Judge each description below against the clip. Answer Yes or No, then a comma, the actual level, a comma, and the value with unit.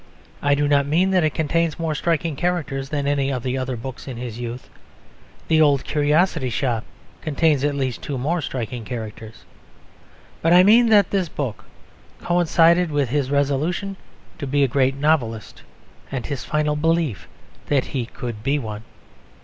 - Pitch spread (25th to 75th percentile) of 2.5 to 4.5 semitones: Yes, average, 4.0 semitones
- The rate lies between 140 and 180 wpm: Yes, average, 165 wpm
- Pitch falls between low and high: Yes, medium, 145 Hz